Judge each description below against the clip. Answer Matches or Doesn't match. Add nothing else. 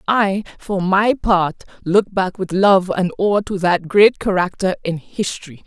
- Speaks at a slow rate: Doesn't match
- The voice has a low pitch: Doesn't match